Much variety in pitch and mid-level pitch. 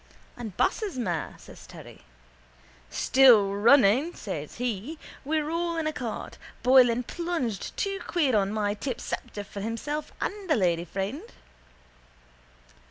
No: wide, 7.5 semitones; high, 235 Hz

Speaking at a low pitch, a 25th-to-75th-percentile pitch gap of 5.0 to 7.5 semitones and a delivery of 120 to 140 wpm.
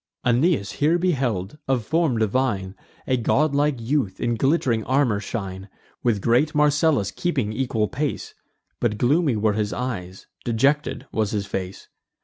Yes: low, 120 Hz; wide, 5.5 semitones; slow, 135 wpm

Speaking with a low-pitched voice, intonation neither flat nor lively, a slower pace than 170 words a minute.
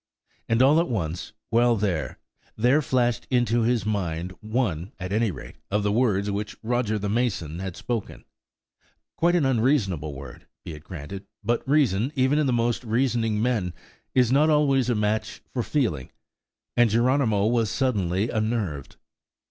Yes: low, 115 Hz; average, 4.2 semitones; average, 155 wpm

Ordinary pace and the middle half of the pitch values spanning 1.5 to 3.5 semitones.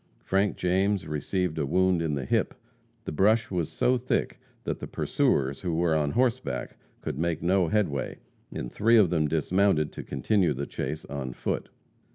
No: average, 175 wpm; average, 4.7 semitones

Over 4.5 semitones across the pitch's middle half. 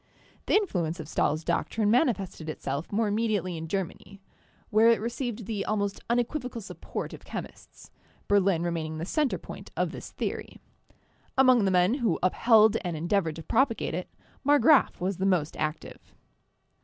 Yes: average, 5.3 semitones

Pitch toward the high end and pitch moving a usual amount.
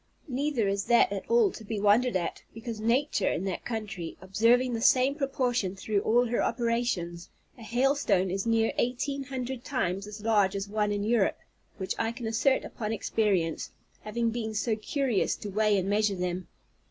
Yes: high, 220 Hz; average, 3.5 semitones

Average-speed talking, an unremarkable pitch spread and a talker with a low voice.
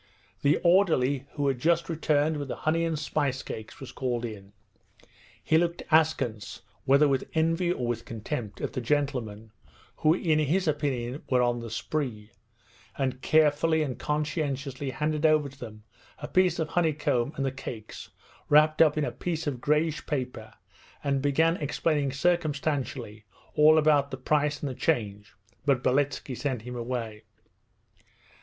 No: average, 155 wpm; average, 3.8 semitones; medium, 145 Hz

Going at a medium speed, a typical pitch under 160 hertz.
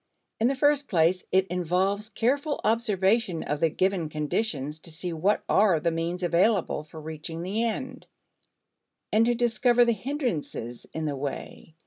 No: average, 155 wpm; medium, 185 Hz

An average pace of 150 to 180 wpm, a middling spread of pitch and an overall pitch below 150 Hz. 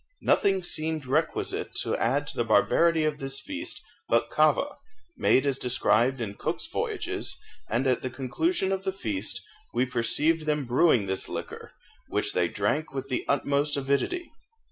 Yes: average, 160 wpm; average, 4.5 semitones; medium, 140 Hz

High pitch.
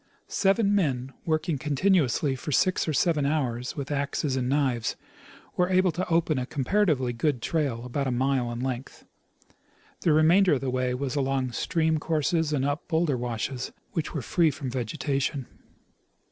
No: medium, 140 Hz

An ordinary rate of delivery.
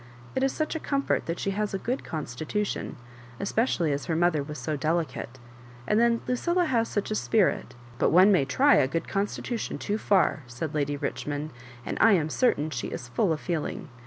No: fast, 215 wpm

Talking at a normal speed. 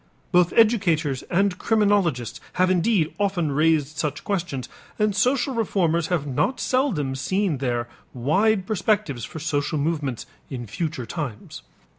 No: slow, 130 wpm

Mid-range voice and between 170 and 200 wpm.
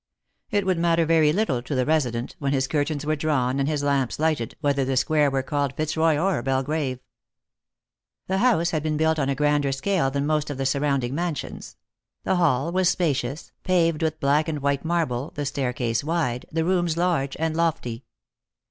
Yes: medium, 150 Hz; average, 185 wpm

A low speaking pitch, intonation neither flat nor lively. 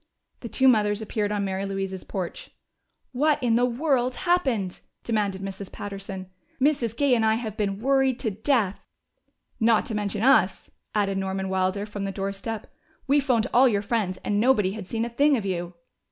No: high, 215 Hz; average, 4.1 semitones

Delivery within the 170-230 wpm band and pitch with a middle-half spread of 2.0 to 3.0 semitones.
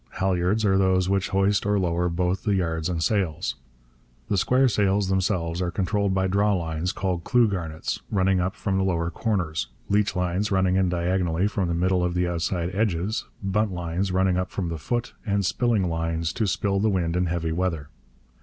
Yes: average, 180 wpm; narrow, 2.4 semitones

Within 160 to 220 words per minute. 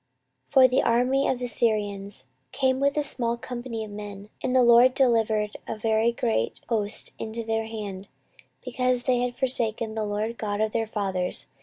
Yes: average, 180 wpm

